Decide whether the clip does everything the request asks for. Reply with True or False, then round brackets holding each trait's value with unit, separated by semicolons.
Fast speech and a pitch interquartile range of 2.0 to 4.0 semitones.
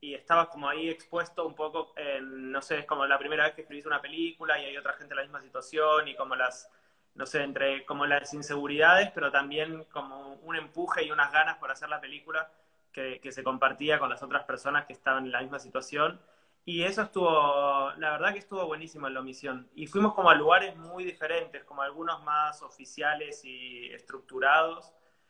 True (205 wpm; 2.9 semitones)